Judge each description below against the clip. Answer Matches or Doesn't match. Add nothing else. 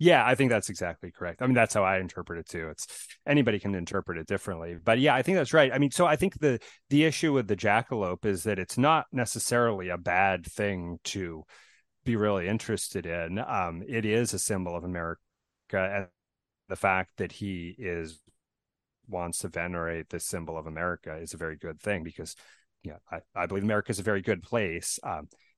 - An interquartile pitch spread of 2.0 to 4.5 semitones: Doesn't match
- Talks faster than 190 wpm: Matches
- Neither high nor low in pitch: Doesn't match